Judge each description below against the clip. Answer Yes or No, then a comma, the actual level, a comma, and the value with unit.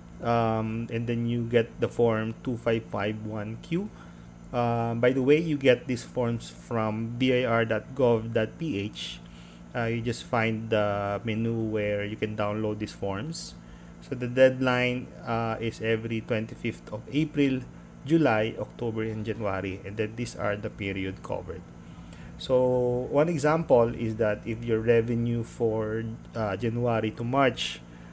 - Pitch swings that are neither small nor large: No, narrow, 2.3 semitones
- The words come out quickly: No, slow, 135 wpm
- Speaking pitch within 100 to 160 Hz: Yes, low, 115 Hz